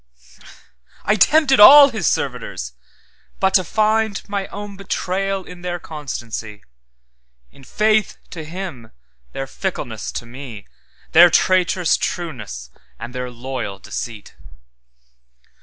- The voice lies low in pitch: No, medium, 160 Hz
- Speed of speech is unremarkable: No, slow, 100 wpm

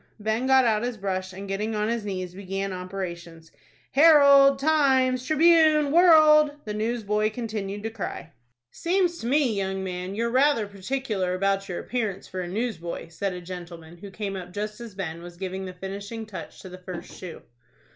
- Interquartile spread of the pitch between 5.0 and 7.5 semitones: Yes, average, 5.3 semitones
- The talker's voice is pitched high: Yes, high, 205 Hz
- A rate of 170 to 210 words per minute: Yes, average, 175 wpm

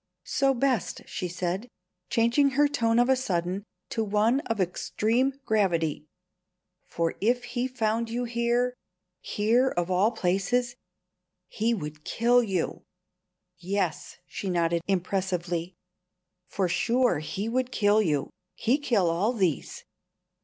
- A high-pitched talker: Yes, high, 215 Hz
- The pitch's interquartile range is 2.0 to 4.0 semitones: No, average, 5.2 semitones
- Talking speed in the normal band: No, slow, 125 wpm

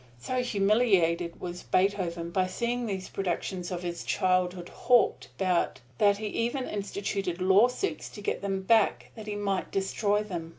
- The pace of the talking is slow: No, average, 155 wpm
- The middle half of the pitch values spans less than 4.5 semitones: Yes, average, 2.8 semitones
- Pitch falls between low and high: No, high, 195 Hz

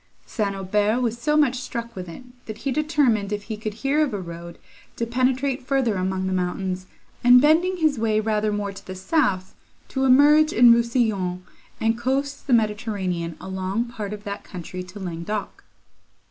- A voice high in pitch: Yes, high, 220 Hz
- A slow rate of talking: No, average, 175 wpm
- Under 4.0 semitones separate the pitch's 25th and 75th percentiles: No, average, 5.1 semitones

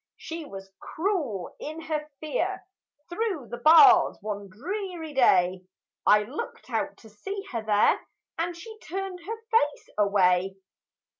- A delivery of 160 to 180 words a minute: No, slow, 135 wpm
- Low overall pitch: No, very high, 300 Hz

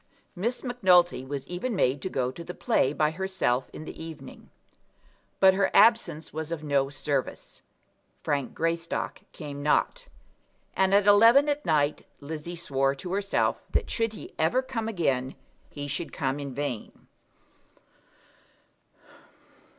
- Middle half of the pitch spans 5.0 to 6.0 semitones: Yes, wide, 5.6 semitones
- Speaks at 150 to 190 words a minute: No, average, 140 wpm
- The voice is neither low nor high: Yes, medium, 165 Hz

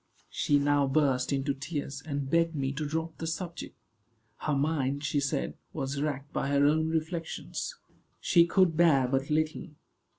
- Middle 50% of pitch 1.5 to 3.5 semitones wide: Yes, narrow, 2.6 semitones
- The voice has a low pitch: No, medium, 145 Hz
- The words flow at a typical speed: Yes, average, 160 wpm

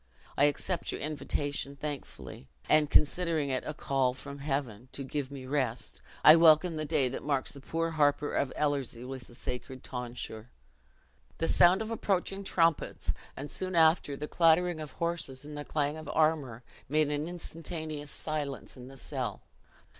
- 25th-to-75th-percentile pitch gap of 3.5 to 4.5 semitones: No, average, 2.9 semitones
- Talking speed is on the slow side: No, average, 165 wpm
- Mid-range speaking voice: Yes, medium, 145 Hz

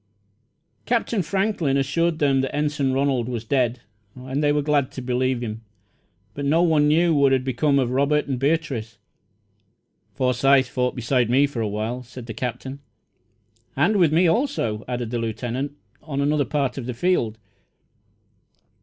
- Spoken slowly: No, average, 160 wpm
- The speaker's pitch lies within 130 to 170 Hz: Yes, low, 135 Hz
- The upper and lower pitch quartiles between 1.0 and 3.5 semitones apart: Yes, average, 3.2 semitones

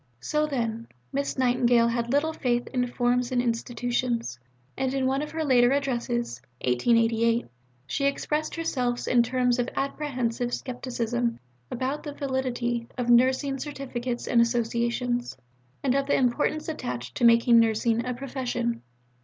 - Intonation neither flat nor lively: No, narrow, 2.1 semitones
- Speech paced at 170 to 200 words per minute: No, average, 140 wpm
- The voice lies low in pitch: No, high, 245 Hz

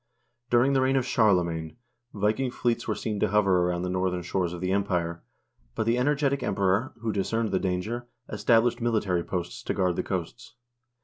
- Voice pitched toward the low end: Yes, low, 100 Hz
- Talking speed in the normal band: Yes, average, 180 wpm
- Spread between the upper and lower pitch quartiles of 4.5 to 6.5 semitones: Yes, average, 4.8 semitones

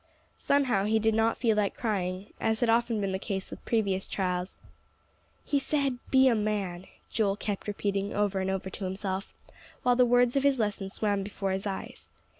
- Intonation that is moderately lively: Yes, average, 3.2 semitones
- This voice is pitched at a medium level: No, high, 205 Hz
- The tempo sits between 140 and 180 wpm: No, average, 190 wpm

